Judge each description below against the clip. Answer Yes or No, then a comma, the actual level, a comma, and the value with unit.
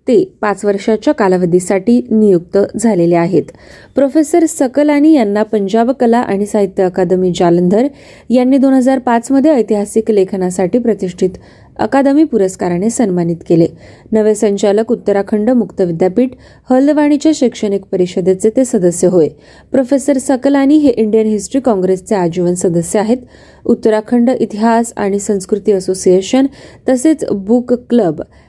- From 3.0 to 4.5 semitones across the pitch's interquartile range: No, average, 4.9 semitones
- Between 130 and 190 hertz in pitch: No, high, 220 Hz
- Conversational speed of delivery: Yes, average, 115 wpm